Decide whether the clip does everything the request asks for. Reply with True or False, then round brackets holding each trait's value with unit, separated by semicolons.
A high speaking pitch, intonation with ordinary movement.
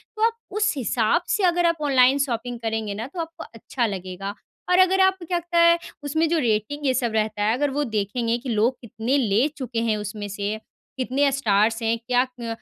False (245 Hz; 6.8 semitones)